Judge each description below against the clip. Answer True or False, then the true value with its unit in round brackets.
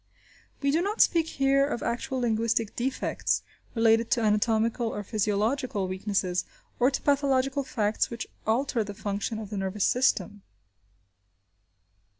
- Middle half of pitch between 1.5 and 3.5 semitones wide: False (4.3 semitones)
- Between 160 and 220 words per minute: False (135 wpm)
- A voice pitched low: False (230 Hz)